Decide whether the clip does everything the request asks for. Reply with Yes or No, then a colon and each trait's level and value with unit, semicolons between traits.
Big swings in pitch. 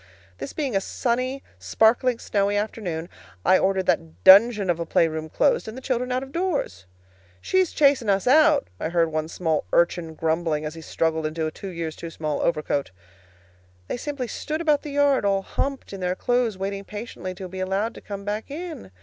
Yes: wide, 7.4 semitones